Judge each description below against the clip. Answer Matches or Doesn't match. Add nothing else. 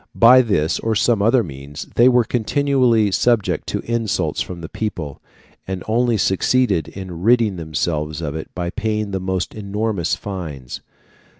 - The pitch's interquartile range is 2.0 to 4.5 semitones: Doesn't match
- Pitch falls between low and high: Doesn't match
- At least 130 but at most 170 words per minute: Matches